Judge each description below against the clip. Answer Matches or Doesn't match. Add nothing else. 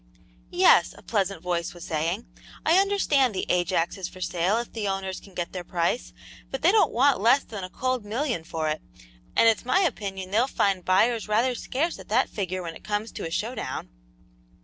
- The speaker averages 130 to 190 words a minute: Doesn't match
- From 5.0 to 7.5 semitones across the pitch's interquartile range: Matches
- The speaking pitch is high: Matches